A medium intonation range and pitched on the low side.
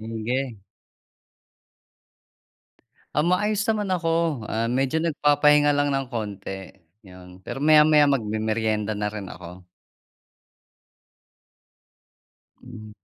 No: wide, 5.8 semitones; low, 125 Hz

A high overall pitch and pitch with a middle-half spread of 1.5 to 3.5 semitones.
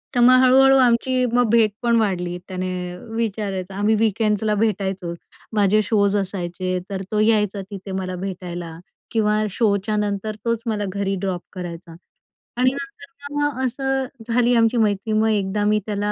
Yes: high, 210 Hz; average, 3.2 semitones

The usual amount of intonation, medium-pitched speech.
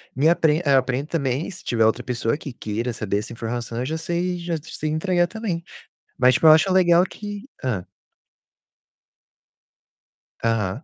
No: wide, 6.5 semitones; medium, 145 Hz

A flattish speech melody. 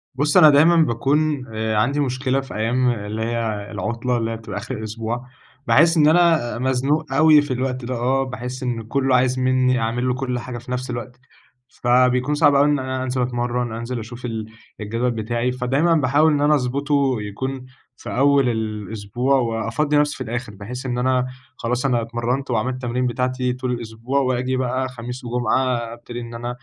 Yes: narrow, 2.2 semitones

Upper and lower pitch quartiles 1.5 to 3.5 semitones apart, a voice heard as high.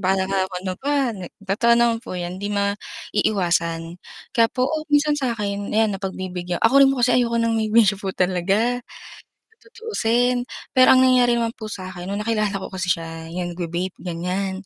No: average, 4.5 semitones; high, 205 Hz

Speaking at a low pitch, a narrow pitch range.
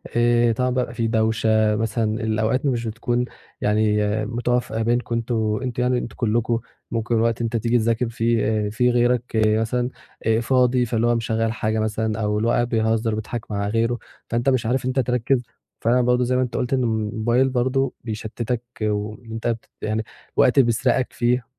Yes: low, 115 Hz; narrow, 1.8 semitones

